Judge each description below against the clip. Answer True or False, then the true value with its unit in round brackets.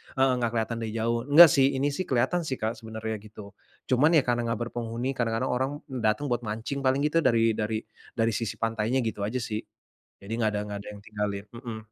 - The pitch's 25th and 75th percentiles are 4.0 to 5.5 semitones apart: False (3.0 semitones)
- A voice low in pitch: True (115 Hz)